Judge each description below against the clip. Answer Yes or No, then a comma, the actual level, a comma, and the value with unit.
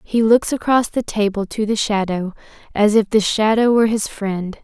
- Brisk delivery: No, average, 195 wpm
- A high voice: Yes, high, 215 Hz